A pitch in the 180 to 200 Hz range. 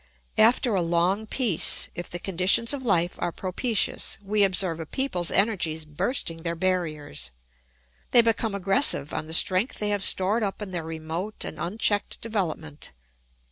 Yes: medium, 185 Hz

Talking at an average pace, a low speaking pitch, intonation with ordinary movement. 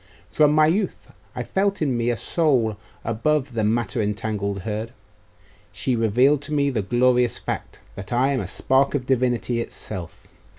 Yes: average, 165 wpm; low, 120 Hz; average, 4.3 semitones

